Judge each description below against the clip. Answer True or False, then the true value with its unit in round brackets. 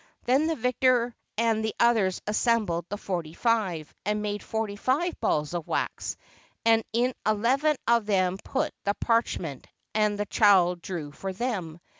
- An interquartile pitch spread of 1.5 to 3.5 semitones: False (4.1 semitones)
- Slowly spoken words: False (160 wpm)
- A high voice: True (210 Hz)